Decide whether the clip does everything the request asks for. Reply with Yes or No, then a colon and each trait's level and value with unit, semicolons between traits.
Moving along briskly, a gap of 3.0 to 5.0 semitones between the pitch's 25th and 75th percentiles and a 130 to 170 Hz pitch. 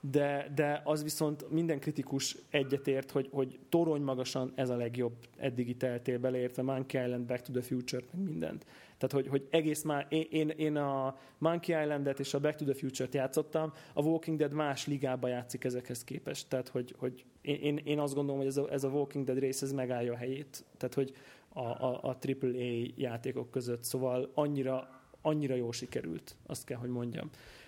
No: fast, 185 wpm; narrow, 2.4 semitones; low, 135 Hz